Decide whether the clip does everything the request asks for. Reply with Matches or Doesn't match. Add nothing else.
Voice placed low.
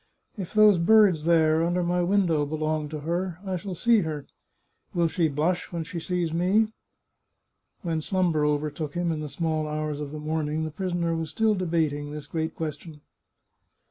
Doesn't match